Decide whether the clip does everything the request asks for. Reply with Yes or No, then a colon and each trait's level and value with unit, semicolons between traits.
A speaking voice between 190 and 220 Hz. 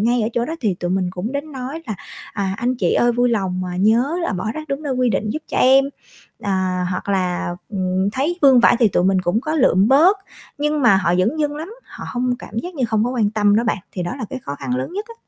No: high, 230 Hz